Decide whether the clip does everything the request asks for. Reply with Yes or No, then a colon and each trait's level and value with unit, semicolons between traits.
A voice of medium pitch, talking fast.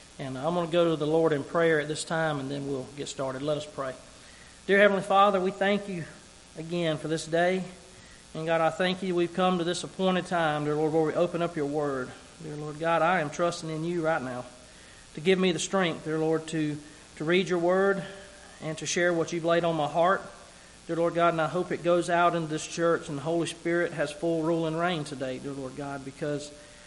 Yes: medium, 165 Hz; fast, 240 wpm